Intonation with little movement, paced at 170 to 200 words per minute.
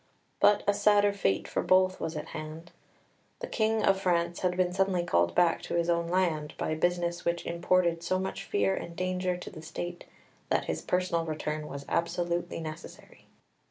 Yes: narrow, 1.9 semitones; average, 180 wpm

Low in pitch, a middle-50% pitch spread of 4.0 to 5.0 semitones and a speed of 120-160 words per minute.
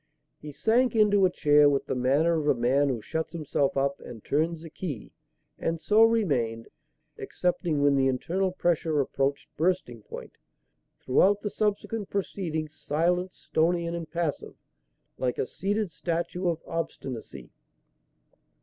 No: medium, 160 Hz; average, 4.6 semitones; average, 140 wpm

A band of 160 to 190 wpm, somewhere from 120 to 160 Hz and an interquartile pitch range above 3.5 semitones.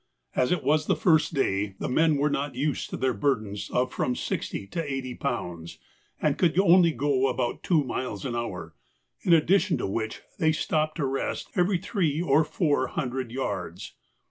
Yes: average, 180 wpm; low, 135 Hz; average, 4.7 semitones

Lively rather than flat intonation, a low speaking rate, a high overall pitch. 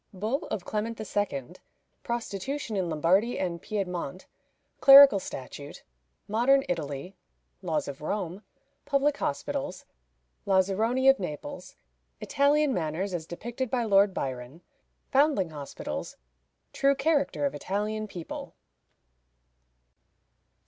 Yes: wide, 7.7 semitones; slow, 100 wpm; high, 205 Hz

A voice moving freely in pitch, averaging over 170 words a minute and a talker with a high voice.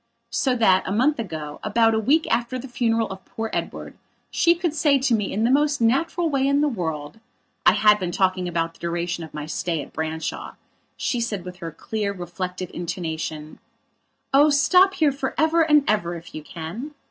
Yes: wide, 8.0 semitones; average, 190 wpm; high, 215 Hz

